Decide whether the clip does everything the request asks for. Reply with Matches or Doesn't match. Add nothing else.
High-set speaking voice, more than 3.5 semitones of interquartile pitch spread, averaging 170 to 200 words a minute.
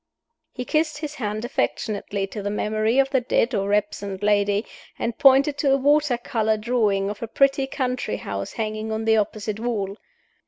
Matches